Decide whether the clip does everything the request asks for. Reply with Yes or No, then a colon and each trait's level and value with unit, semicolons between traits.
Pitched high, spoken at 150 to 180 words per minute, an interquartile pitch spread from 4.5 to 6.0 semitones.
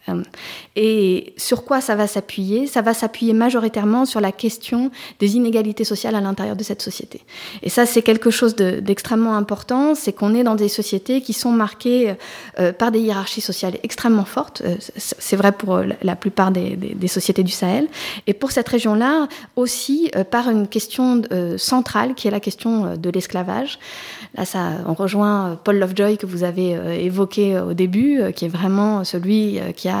No: high, 215 Hz; average, 170 wpm; average, 3.5 semitones